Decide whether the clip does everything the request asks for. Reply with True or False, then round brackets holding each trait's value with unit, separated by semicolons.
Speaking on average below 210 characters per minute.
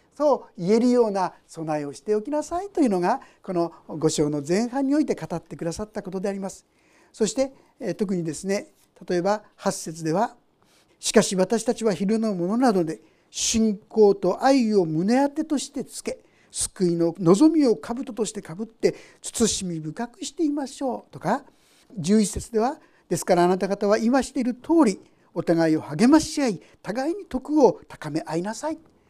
False (330 characters per minute)